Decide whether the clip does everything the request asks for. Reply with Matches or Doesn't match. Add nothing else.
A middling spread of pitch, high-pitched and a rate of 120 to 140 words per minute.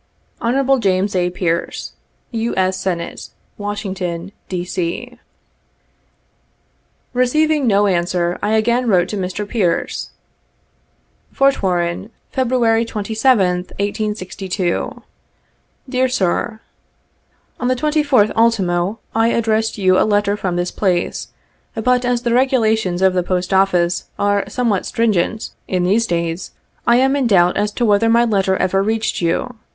Matches